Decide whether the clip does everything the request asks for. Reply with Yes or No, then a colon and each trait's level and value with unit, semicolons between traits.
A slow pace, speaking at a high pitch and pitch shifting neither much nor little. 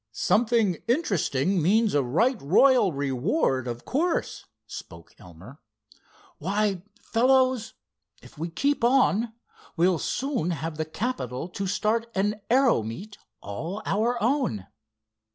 No: slow, 115 wpm; high, 200 Hz; wide, 8.1 semitones